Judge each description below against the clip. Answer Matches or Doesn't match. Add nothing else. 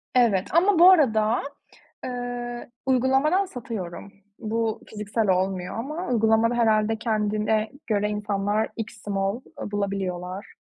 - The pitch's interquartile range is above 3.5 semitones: Doesn't match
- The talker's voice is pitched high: Matches